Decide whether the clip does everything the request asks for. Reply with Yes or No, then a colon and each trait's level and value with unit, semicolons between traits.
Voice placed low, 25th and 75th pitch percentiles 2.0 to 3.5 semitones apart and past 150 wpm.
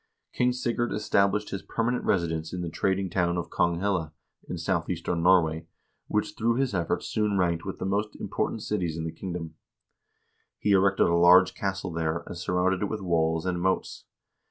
Yes: very low, 90 Hz; average, 2.8 semitones; average, 175 wpm